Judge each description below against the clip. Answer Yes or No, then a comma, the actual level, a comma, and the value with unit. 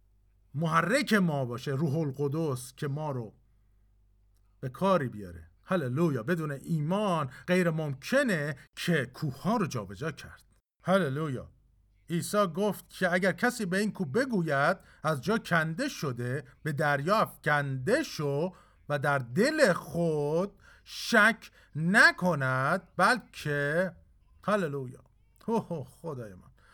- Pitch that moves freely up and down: Yes, wide, 5.8 semitones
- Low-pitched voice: No, medium, 155 Hz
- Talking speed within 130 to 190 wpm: No, average, 115 wpm